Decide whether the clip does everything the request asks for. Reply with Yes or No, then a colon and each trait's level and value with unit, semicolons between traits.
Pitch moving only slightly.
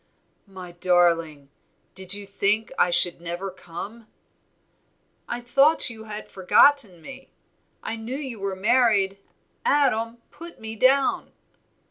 No: average, 5.0 semitones